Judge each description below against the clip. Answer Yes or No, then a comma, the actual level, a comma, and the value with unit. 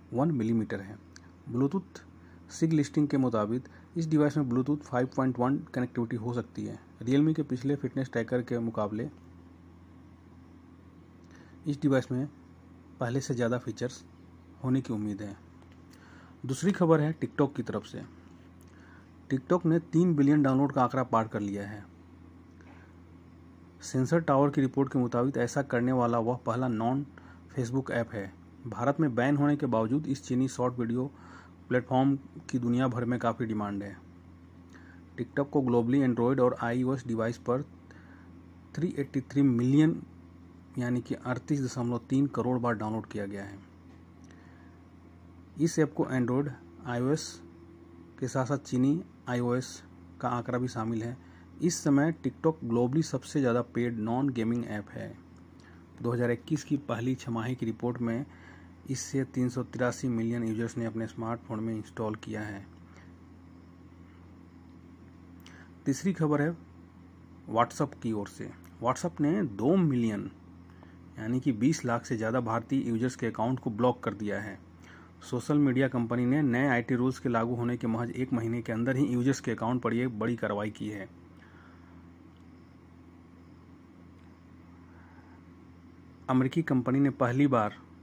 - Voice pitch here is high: No, low, 115 Hz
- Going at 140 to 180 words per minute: Yes, average, 145 wpm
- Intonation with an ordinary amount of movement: No, wide, 6.8 semitones